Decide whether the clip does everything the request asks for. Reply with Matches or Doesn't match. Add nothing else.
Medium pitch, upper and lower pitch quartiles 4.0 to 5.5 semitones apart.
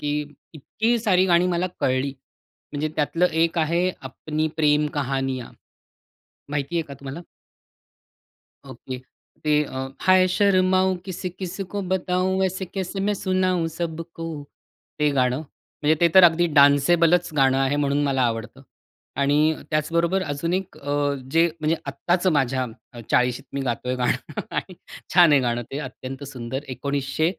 Matches